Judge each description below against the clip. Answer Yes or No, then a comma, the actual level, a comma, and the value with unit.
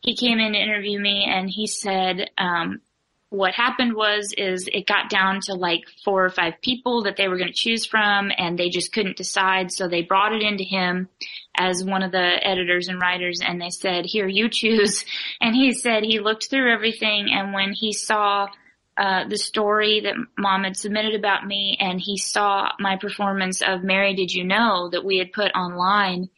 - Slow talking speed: No, average, 200 wpm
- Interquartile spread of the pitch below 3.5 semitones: Yes, narrow, 2.4 semitones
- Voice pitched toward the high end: Yes, high, 200 Hz